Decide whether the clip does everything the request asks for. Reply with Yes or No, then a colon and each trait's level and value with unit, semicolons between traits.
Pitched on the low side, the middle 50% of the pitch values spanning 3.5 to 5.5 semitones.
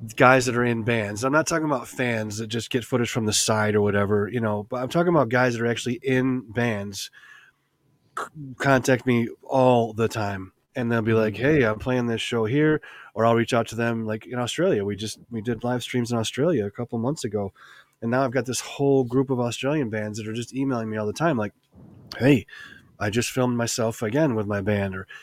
No: low, 120 Hz; average, 2.9 semitones